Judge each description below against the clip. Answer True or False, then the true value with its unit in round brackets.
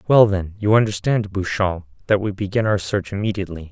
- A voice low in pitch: True (100 Hz)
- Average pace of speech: True (180 wpm)